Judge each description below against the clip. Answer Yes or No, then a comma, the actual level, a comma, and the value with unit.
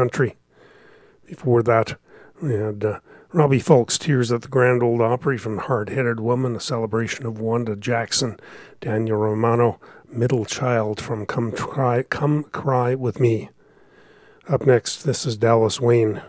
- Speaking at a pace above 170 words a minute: No, average, 145 wpm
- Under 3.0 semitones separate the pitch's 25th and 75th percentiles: Yes, narrow, 2.5 semitones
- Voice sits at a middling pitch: No, low, 120 Hz